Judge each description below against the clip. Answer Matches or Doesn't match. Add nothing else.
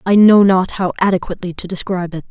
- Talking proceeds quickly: Matches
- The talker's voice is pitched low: Doesn't match